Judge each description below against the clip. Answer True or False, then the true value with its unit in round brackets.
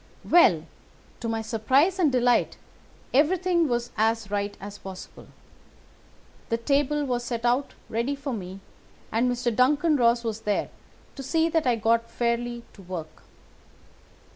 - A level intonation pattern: False (4.0 semitones)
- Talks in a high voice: True (240 Hz)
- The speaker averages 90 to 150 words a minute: True (140 wpm)